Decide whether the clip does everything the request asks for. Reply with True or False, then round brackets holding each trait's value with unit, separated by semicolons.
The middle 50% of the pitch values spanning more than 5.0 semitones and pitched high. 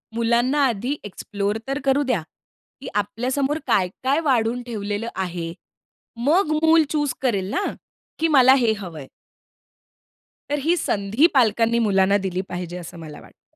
True (5.5 semitones; 230 Hz)